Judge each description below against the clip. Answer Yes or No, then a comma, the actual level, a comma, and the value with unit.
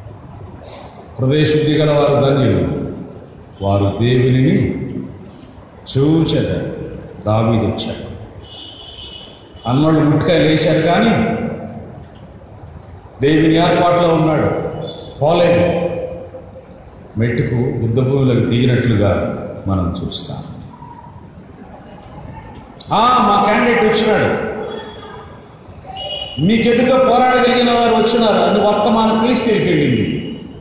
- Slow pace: Yes, slow, 60 wpm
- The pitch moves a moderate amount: No, wide, 8.4 semitones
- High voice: No, medium, 140 Hz